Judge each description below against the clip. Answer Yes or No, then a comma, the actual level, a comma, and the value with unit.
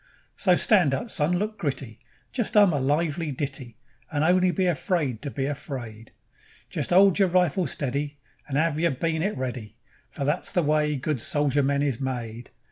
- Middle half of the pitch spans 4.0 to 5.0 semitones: Yes, average, 4.6 semitones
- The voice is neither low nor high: Yes, medium, 145 Hz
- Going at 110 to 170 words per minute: No, average, 180 wpm